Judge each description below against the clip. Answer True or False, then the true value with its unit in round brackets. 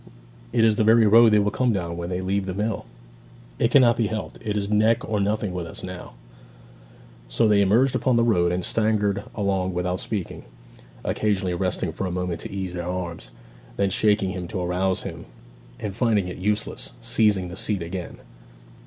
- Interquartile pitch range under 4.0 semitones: True (3.0 semitones)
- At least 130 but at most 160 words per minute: False (190 wpm)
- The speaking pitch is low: True (100 Hz)